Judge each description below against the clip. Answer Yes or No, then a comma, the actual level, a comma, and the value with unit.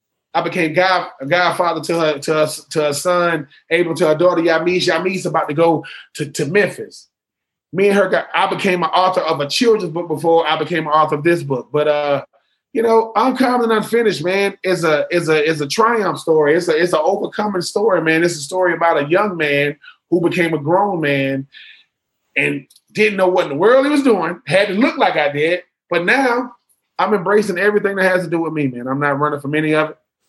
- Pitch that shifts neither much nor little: Yes, average, 4.0 semitones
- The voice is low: No, medium, 175 Hz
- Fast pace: Yes, fast, 225 wpm